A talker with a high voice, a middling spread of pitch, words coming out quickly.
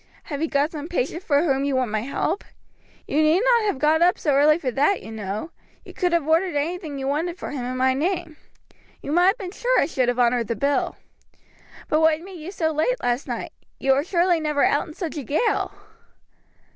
Yes: very high, 305 Hz; average, 4.2 semitones; fast, 225 wpm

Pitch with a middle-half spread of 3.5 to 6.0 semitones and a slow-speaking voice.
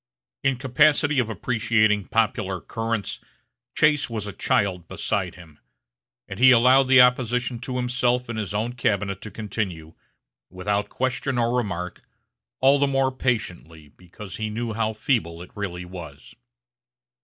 No: average, 4.4 semitones; average, 145 wpm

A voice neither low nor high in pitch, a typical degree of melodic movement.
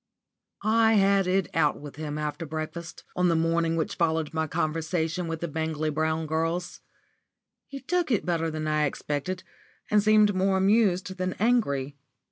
Yes: medium, 165 Hz; average, 3.4 semitones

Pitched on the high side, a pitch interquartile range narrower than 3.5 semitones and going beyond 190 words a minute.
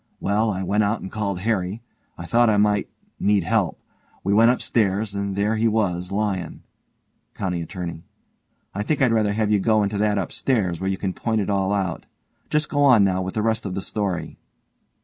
No: low, 100 Hz; narrow, 2.5 semitones; average, 200 wpm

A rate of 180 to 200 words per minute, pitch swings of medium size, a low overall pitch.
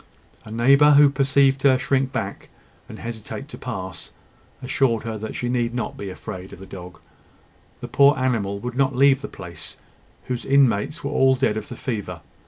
Yes: average, 185 wpm; average, 4.3 semitones; low, 125 Hz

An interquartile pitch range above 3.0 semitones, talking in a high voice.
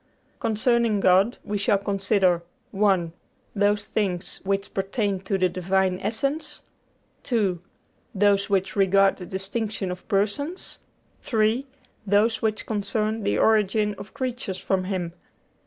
No: narrow, 2.4 semitones; high, 200 Hz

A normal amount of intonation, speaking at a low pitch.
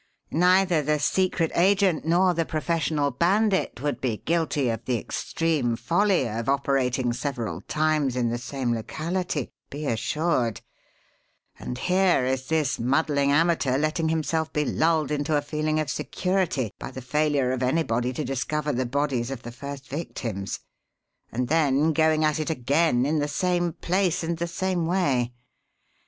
No: average, 4.3 semitones; medium, 150 Hz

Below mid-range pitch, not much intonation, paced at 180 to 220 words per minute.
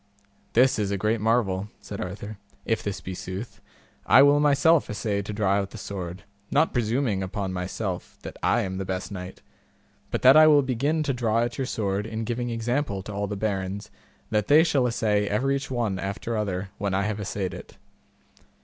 No: low, 105 Hz; average, 3.9 semitones; average, 195 wpm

